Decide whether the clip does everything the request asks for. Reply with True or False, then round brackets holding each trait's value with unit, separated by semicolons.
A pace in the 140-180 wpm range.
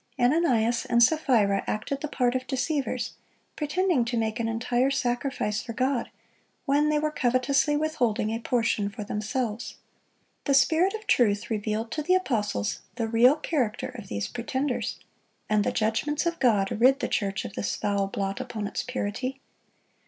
True (160 wpm)